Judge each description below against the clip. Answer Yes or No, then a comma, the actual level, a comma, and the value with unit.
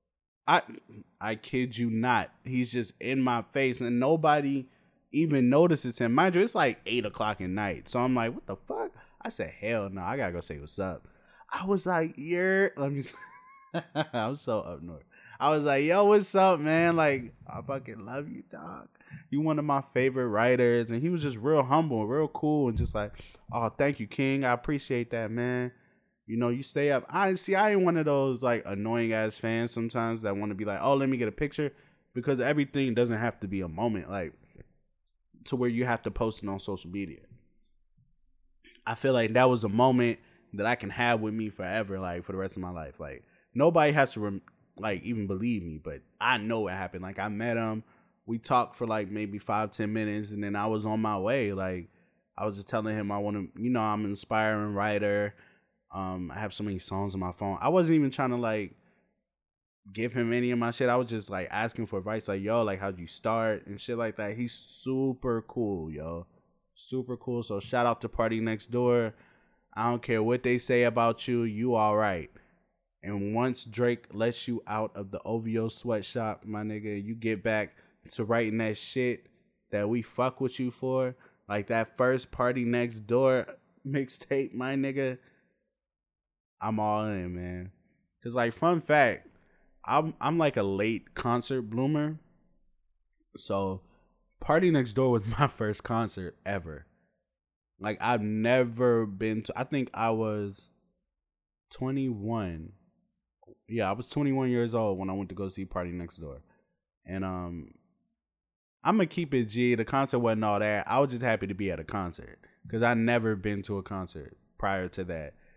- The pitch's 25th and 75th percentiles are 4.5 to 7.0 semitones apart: No, average, 3.9 semitones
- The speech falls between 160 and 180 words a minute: No, average, 195 wpm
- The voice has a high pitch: No, low, 115 Hz